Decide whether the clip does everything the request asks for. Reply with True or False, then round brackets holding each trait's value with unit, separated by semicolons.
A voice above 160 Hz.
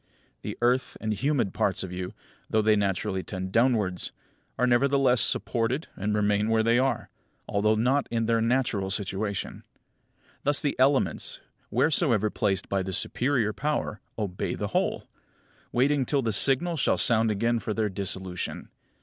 False (110 Hz)